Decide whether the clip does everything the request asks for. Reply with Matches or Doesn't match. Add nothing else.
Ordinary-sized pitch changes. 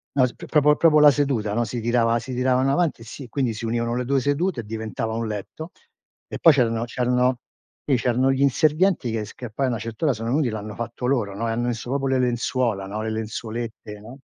Matches